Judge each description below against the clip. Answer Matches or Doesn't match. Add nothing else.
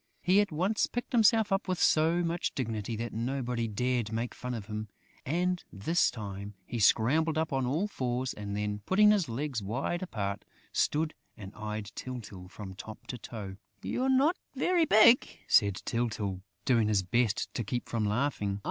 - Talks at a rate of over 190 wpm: Doesn't match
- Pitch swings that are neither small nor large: Doesn't match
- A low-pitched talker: Matches